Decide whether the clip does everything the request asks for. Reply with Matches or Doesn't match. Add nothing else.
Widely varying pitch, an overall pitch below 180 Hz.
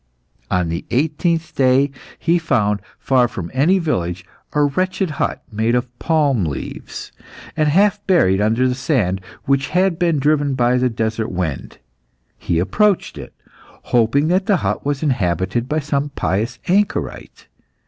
Matches